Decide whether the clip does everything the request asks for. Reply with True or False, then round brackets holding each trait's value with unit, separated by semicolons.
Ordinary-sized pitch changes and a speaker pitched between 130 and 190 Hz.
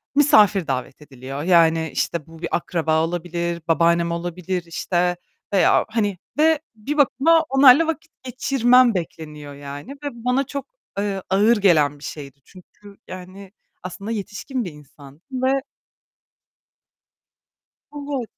False (7.4 semitones; 185 Hz)